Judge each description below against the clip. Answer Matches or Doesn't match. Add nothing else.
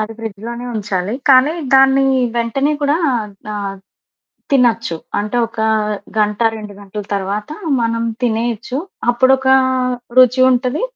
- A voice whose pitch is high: Matches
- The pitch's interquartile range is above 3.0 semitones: Matches